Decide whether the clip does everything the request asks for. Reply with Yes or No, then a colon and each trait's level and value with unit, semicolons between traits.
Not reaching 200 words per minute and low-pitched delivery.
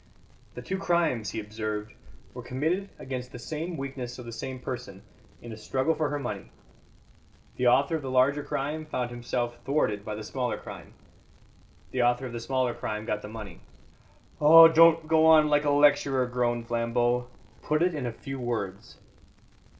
Yes: average, 175 wpm; low, 130 Hz